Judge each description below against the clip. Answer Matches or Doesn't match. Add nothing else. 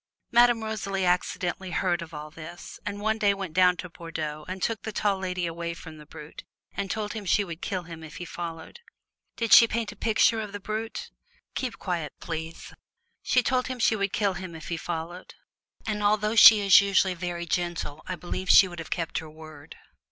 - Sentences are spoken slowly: Doesn't match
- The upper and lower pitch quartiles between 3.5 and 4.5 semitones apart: Matches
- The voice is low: Doesn't match